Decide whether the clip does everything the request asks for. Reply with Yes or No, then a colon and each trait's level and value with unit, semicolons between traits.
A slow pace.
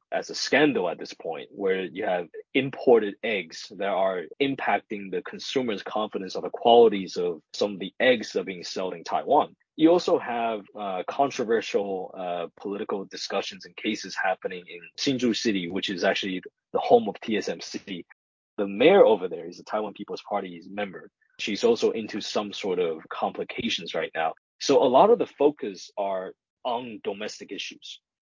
No: average, 175 wpm